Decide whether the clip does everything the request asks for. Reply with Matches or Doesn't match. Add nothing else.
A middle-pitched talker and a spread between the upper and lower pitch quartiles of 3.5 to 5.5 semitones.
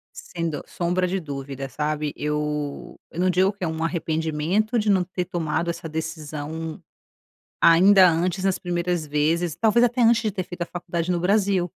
Doesn't match